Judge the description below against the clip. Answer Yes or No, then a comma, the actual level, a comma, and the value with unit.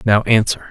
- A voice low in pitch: Yes, low, 110 Hz